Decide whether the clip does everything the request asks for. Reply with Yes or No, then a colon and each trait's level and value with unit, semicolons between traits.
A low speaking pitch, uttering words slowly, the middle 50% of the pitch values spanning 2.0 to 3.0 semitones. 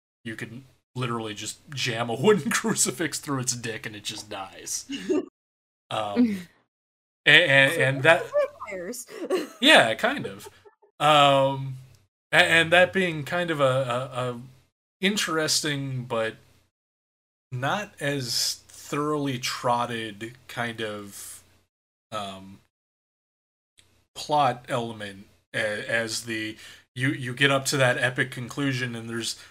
No: low, 125 Hz; slow, 115 wpm; average, 5.0 semitones